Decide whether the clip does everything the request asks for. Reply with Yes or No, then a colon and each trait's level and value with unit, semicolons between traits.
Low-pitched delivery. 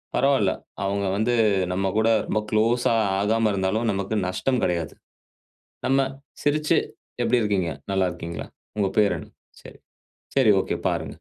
Yes: low, 105 Hz